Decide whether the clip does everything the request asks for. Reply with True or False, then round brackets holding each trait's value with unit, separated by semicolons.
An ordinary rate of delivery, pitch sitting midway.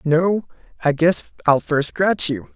True (165 wpm; 160 Hz)